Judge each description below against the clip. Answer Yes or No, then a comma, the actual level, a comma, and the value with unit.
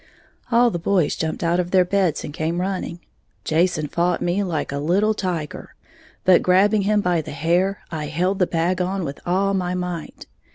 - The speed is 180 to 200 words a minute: Yes, average, 190 wpm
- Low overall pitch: No, medium, 180 Hz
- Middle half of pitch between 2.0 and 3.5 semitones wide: Yes, narrow, 2.5 semitones